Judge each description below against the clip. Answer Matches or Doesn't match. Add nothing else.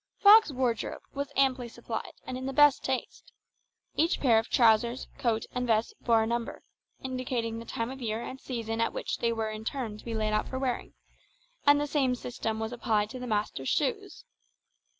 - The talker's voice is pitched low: Doesn't match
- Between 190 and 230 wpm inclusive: Matches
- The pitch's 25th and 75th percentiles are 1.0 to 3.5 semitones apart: Matches